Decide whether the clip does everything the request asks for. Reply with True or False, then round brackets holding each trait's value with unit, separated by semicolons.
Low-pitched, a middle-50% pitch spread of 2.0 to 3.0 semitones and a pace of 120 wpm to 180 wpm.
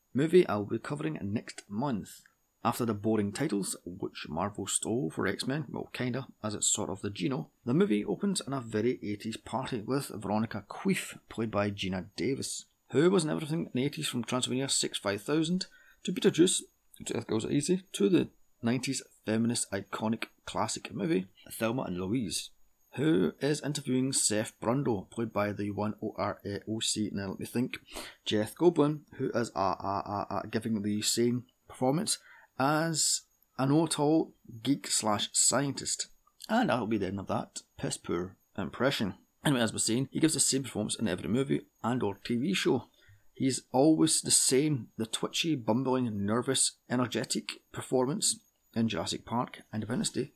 False (115 Hz; 4.6 semitones; 165 wpm)